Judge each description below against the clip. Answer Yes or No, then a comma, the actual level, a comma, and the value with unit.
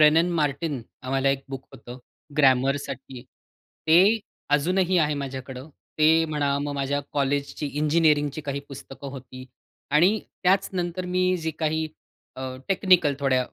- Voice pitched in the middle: Yes, medium, 145 Hz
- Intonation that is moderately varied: Yes, average, 3.2 semitones